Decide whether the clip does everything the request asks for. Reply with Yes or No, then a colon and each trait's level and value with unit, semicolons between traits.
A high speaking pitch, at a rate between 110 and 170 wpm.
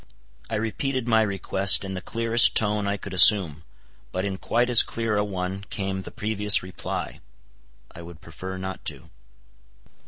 No: low, 100 Hz; average, 160 wpm